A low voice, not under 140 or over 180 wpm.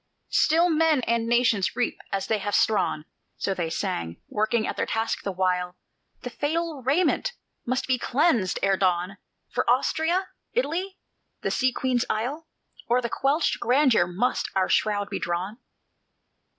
No: high, 235 Hz; average, 150 wpm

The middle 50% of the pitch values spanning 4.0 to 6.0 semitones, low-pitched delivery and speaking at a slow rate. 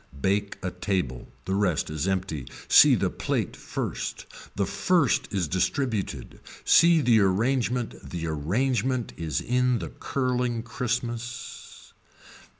Yes: wide, 5.4 semitones; low, 110 Hz; slow, 120 wpm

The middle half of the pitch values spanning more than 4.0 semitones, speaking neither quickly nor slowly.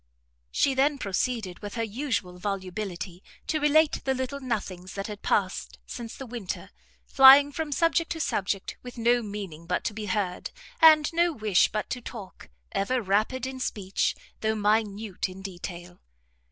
Yes: wide, 5.4 semitones; average, 160 wpm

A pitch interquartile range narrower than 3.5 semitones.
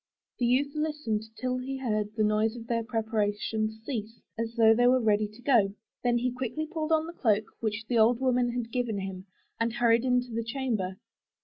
Yes: narrow, 2.5 semitones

